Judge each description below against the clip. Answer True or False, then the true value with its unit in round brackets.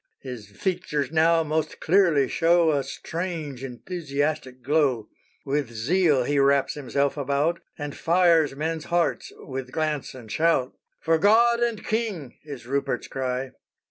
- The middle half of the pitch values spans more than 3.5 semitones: True (3.9 semitones)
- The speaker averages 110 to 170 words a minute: True (140 wpm)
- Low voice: False (150 Hz)